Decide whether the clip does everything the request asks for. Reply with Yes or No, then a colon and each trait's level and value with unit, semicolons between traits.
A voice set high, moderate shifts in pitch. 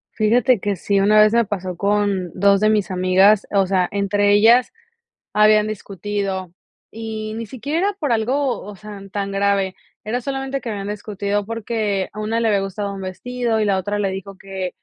No: high, 205 Hz; narrow, 2.0 semitones